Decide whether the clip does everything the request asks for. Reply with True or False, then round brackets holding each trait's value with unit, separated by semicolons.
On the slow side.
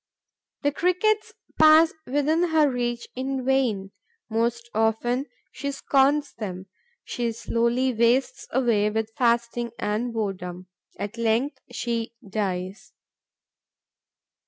True (105 wpm)